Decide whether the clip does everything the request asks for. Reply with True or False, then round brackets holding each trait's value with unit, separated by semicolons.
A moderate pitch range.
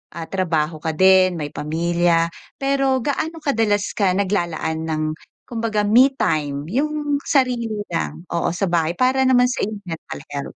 False (7.2 semitones)